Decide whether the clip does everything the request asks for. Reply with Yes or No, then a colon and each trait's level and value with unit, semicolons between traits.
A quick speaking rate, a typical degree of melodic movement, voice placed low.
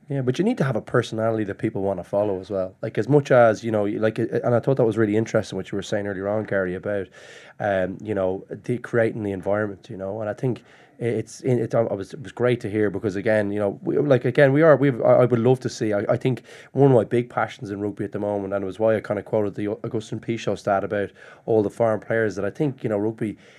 Yes: fast, 285 wpm; average, 3.0 semitones; low, 110 Hz